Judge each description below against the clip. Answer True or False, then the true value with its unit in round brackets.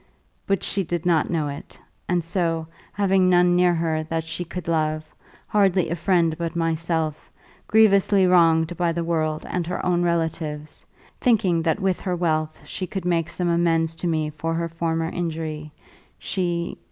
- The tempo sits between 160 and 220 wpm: True (165 wpm)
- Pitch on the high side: False (170 Hz)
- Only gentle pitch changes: True (1.7 semitones)